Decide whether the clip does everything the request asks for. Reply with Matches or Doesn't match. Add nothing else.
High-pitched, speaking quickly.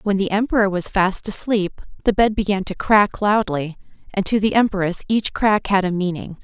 Doesn't match